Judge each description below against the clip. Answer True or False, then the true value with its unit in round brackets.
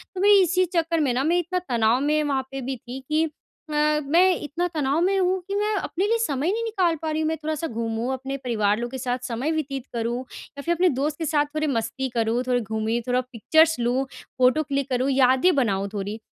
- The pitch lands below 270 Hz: False (275 Hz)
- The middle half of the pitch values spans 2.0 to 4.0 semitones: False (4.7 semitones)